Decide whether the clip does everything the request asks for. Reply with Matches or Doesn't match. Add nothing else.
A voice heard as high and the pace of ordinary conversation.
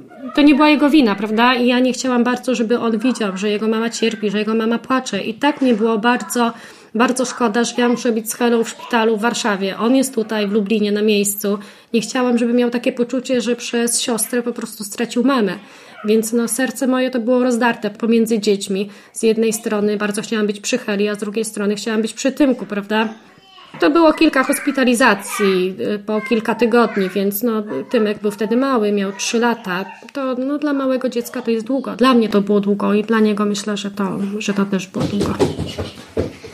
Doesn't match